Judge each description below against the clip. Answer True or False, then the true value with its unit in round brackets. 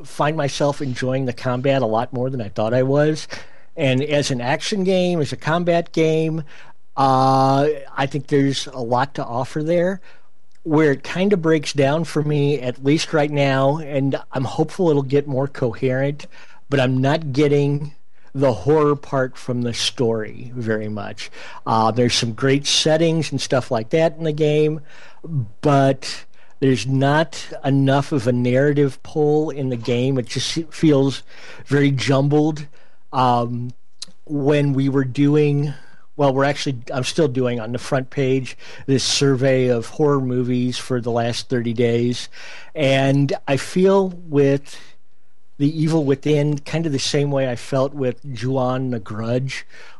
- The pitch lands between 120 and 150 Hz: True (135 Hz)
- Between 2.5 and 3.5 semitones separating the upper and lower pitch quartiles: True (2.8 semitones)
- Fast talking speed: False (160 wpm)